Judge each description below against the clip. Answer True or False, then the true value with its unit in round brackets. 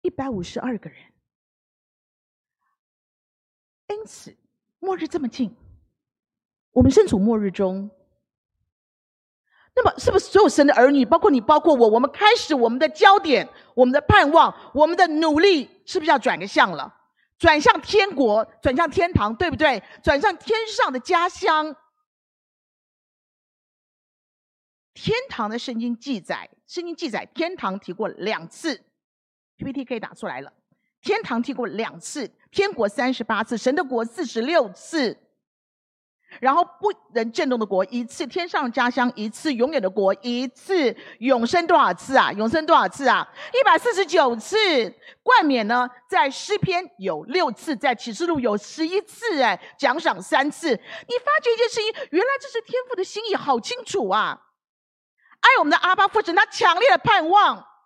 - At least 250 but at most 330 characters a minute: False (230 characters per minute)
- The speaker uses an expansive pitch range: True (8.1 semitones)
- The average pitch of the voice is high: True (300 Hz)